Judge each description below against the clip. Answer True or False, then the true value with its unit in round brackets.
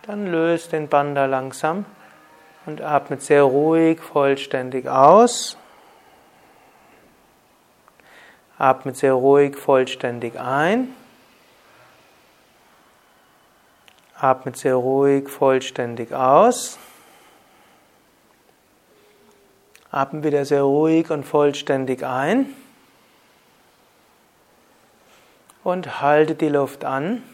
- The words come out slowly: True (70 wpm)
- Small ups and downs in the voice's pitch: False (3.7 semitones)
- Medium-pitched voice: True (145 Hz)